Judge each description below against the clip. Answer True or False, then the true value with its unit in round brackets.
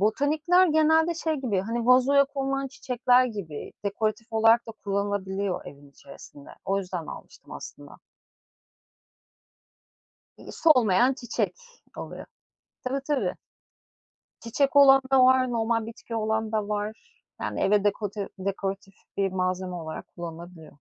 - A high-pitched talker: True (220 Hz)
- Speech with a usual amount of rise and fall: True (5.0 semitones)